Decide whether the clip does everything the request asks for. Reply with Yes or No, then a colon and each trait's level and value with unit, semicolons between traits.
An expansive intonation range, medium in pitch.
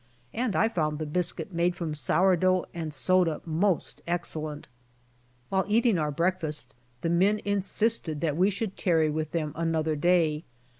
No: average, 3.3 semitones; medium, 170 Hz